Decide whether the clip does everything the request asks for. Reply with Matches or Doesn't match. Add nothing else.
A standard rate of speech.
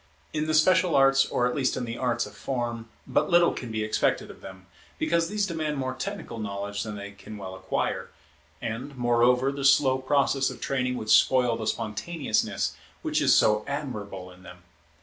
Matches